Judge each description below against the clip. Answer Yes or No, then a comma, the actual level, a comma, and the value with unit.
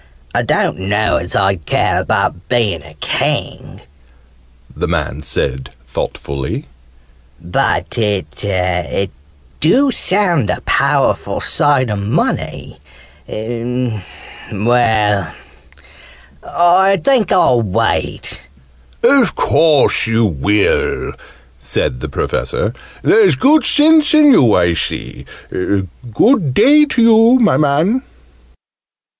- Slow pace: Yes, slow, 100 wpm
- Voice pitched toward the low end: Yes, low, 115 Hz